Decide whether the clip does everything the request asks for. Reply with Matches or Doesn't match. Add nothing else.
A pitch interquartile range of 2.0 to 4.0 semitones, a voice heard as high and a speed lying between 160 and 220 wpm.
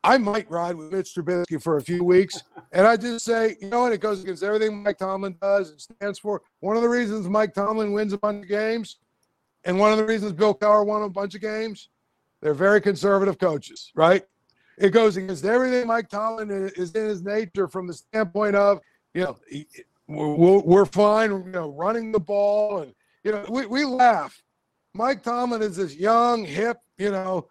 Matches